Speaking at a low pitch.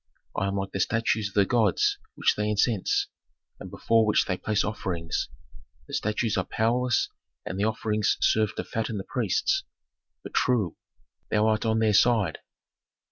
Yes: low, 105 Hz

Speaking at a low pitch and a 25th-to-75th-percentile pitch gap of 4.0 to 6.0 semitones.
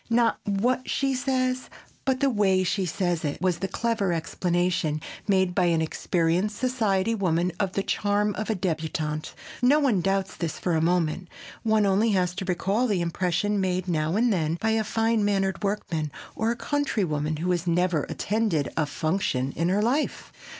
No: high, 190 Hz; average, 4.3 semitones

